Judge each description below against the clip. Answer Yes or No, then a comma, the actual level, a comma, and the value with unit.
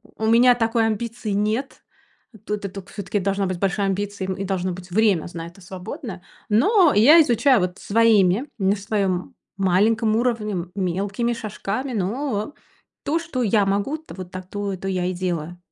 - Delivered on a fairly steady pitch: No, average, 3.5 semitones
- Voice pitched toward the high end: Yes, high, 205 Hz